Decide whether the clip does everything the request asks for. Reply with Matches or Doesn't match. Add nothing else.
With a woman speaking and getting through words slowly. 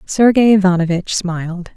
Matches